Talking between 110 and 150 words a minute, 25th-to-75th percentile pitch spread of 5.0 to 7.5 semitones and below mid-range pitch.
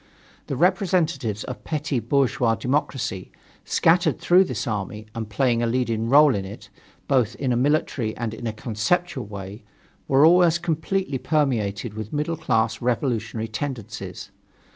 Yes: average, 140 wpm; wide, 5.5 semitones; low, 125 Hz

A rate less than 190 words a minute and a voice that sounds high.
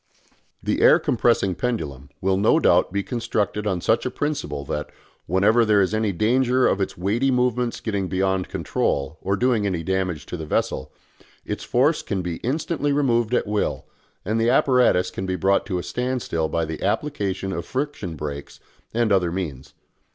No: average, 175 wpm; low, 100 Hz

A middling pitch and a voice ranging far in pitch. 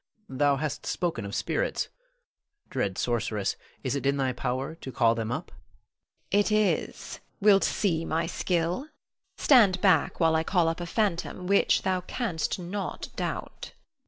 Yes: medium, 165 Hz; wide, 6.3 semitones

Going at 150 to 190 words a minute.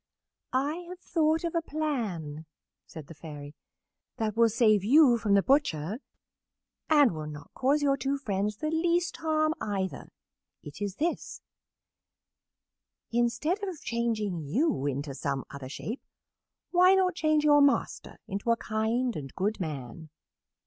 No: average, 140 wpm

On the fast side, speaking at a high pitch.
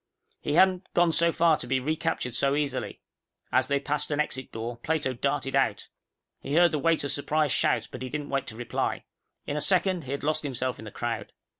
No: fast, 210 wpm; medium, 145 Hz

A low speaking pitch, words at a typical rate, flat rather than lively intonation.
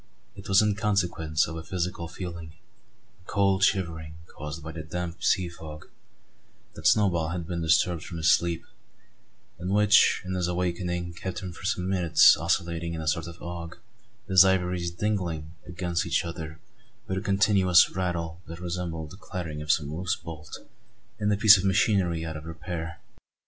Yes: very low, 85 Hz; average, 170 wpm; narrow, 2.3 semitones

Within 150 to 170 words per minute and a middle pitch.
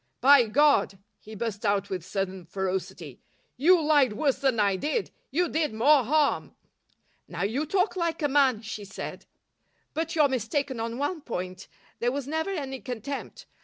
No: average, 165 wpm; very high, 255 Hz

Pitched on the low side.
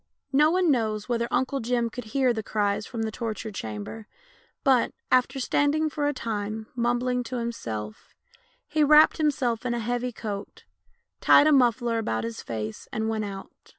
No: high, 235 Hz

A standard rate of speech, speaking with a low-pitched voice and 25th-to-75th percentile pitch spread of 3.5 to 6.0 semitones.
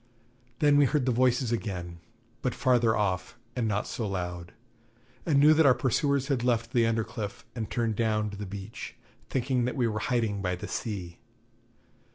Yes: average, 190 wpm; low, 115 Hz; average, 3.8 semitones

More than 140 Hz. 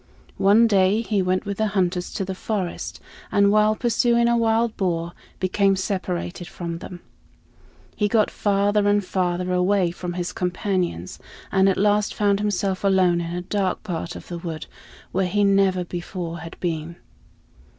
Yes: high, 190 Hz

